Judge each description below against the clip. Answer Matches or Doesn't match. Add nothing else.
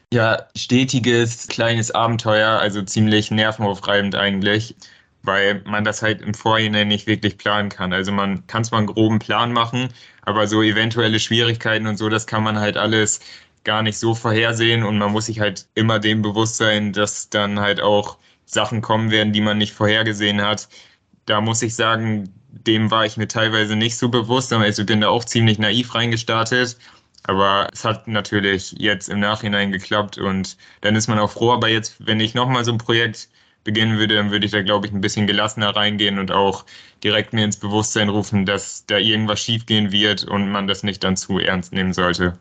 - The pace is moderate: Doesn't match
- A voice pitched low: Matches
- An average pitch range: Doesn't match